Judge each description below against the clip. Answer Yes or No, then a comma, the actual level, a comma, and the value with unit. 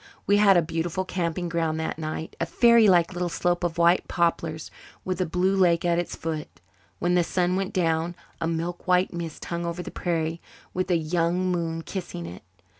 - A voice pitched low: No, medium, 170 Hz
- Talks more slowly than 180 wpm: No, average, 190 wpm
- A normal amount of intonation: No, narrow, 1.7 semitones